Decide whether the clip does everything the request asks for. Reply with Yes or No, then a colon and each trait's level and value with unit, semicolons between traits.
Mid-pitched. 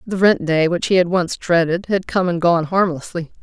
Yes: medium, 175 Hz